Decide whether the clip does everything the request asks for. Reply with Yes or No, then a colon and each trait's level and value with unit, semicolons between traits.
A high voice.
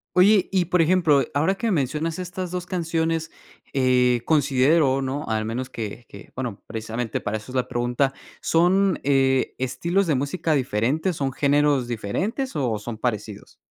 No: medium, 140 Hz